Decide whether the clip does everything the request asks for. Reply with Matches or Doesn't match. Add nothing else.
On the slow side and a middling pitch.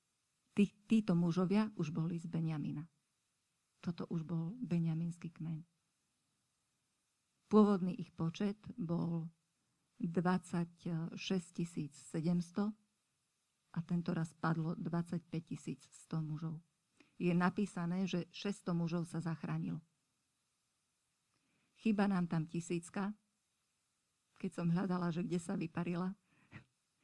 Matches